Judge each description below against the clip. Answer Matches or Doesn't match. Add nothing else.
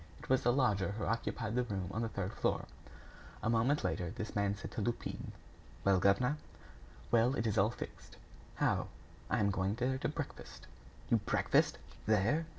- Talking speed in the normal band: Matches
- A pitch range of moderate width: Matches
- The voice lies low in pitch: Matches